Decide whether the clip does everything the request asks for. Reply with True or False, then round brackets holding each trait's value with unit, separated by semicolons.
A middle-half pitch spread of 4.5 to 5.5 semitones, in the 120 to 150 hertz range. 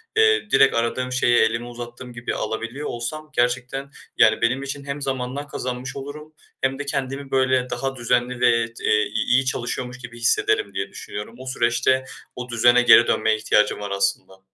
False (2.3 semitones; 125 Hz)